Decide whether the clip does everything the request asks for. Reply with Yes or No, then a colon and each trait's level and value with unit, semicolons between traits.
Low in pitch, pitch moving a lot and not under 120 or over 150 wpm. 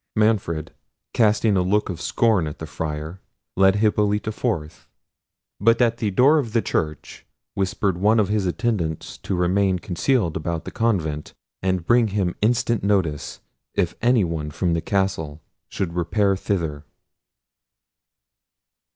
No: very low, 95 Hz; average, 4.5 semitones; average, 140 wpm